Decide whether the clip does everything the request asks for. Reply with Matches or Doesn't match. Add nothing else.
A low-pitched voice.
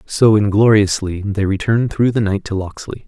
Matches